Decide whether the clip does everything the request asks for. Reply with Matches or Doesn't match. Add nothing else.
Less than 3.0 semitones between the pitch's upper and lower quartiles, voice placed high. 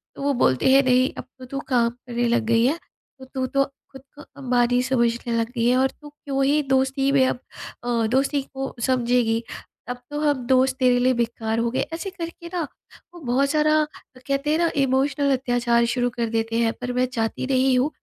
Matches